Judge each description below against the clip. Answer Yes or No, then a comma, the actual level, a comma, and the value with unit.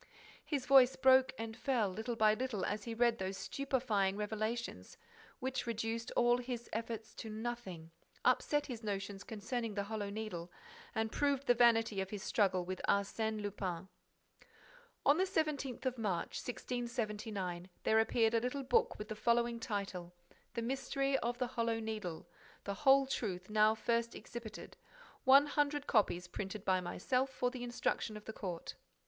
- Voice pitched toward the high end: Yes, high, 225 Hz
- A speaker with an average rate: Yes, average, 160 wpm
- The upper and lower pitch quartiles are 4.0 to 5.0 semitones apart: No, average, 3.4 semitones